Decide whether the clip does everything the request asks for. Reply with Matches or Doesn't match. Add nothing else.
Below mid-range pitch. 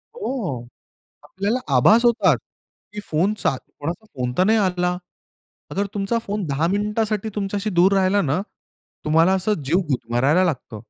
Doesn't match